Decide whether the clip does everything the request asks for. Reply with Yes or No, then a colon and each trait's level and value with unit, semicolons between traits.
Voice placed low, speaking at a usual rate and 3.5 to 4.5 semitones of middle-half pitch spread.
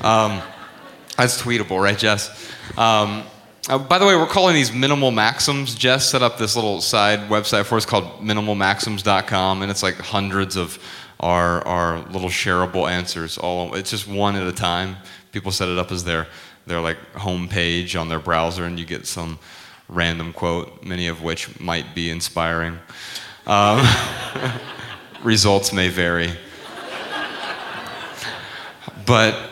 Yes: very low, 95 Hz; average, 145 wpm; average, 4.1 semitones